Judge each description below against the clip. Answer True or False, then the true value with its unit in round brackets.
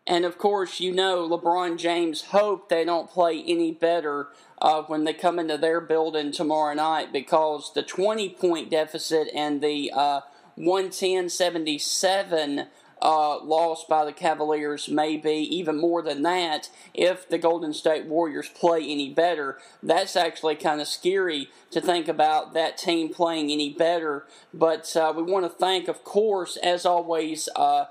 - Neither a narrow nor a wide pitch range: False (2.3 semitones)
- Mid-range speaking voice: True (165 Hz)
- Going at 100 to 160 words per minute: True (155 wpm)